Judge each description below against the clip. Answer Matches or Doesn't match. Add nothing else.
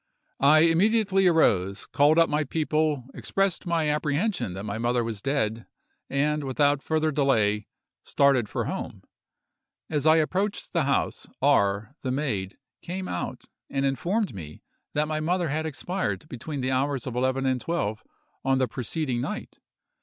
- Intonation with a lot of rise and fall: Doesn't match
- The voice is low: Doesn't match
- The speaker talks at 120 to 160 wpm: Matches